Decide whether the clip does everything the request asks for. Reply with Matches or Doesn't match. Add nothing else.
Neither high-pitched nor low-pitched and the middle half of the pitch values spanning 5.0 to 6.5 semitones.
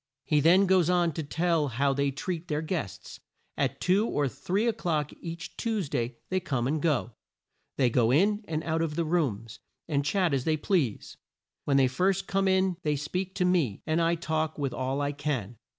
Doesn't match